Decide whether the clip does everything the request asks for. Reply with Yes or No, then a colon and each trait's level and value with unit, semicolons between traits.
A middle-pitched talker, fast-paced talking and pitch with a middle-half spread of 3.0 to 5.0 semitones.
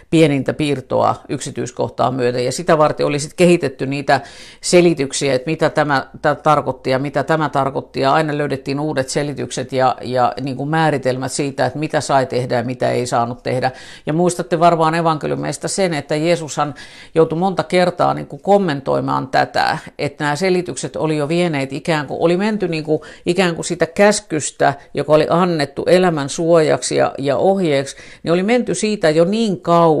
Yes: medium, 155 Hz; fast, 170 wpm; average, 3.9 semitones